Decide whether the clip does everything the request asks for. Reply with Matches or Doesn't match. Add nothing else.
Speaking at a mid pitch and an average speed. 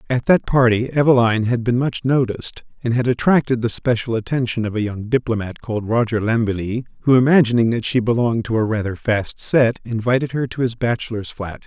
Doesn't match